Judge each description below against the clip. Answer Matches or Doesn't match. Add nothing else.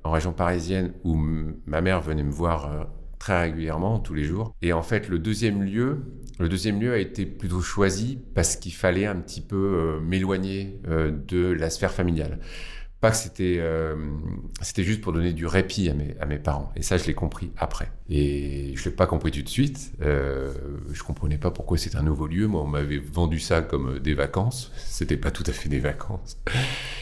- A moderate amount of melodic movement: Matches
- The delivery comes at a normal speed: Matches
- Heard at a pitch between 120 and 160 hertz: Doesn't match